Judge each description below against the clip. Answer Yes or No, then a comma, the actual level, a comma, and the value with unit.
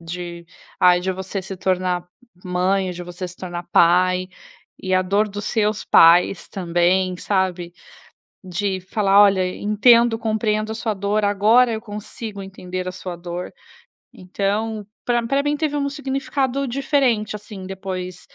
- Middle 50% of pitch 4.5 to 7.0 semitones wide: No, average, 3.1 semitones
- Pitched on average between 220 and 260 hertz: No, high, 195 Hz